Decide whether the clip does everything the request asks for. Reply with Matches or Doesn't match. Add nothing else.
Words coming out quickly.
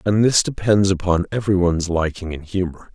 Doesn't match